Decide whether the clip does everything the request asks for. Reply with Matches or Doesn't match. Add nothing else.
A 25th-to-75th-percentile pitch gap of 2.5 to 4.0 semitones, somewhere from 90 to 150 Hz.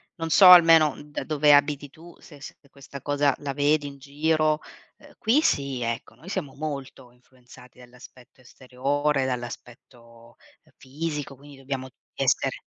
Matches